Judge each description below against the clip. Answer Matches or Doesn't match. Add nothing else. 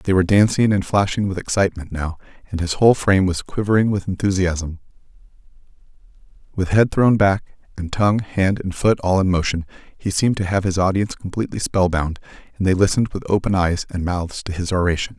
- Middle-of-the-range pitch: Doesn't match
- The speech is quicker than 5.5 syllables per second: Matches